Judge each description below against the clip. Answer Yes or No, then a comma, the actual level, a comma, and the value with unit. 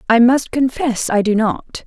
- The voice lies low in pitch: No, high, 240 Hz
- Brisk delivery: No, average, 195 wpm